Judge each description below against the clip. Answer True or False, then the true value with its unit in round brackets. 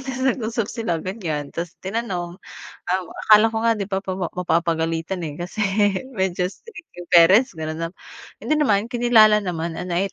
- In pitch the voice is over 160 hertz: True (190 Hz)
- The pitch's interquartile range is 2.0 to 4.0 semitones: False (4.7 semitones)